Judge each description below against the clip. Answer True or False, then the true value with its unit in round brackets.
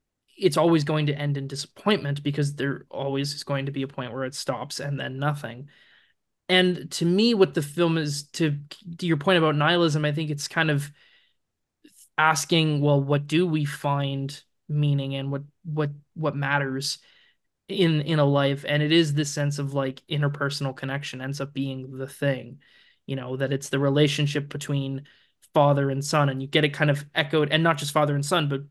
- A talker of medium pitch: True (145 Hz)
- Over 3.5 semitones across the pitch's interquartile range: False (2.4 semitones)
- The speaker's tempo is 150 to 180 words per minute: False (195 wpm)